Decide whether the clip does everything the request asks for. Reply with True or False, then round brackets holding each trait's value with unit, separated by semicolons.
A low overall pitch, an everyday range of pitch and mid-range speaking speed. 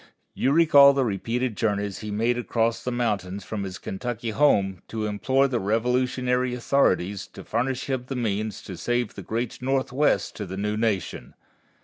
True (115 Hz; 3.6 semitones; 165 wpm)